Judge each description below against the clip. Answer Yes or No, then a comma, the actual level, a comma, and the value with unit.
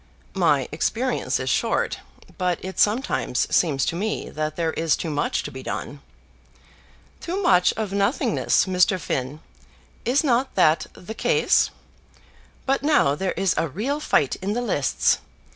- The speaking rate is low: No, average, 150 wpm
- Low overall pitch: No, medium, 185 Hz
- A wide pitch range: Yes, wide, 7.2 semitones